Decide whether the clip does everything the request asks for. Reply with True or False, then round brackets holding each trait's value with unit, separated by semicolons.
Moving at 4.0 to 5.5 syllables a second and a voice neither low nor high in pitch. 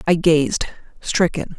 False (3.6 syllables/s; 165 Hz)